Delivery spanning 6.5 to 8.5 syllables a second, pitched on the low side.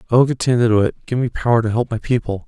Yes: 6.7 syllables/s; low, 120 Hz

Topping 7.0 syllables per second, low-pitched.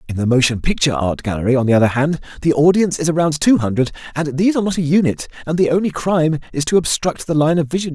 No: 7.2 syllables/s; medium, 150 Hz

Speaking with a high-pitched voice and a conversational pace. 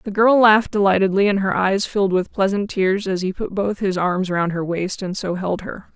No: high, 195 Hz; fast, 240 wpm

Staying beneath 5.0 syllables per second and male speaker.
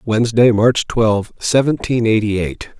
Yes: 4.0 syllables/s; male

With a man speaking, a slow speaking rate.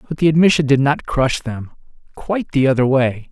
No: male; average, 200 wpm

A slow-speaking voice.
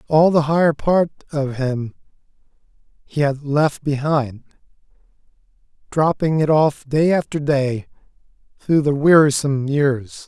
Yes: slow, 115 wpm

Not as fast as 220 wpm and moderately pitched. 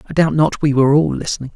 No: fast, 270 wpm; medium, 145 Hz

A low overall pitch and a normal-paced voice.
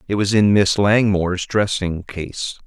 Yes: low, 100 Hz; average, 155 wpm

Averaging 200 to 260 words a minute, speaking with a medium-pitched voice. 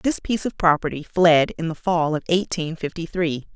Yes: fast, 205 wpm; medium, 165 Hz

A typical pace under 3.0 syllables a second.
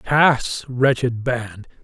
Yes: 2.4 syllables/s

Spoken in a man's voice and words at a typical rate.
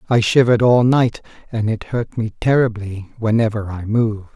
Yes: male; average, 165 wpm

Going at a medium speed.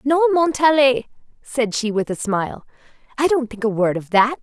Yes: average, 190 wpm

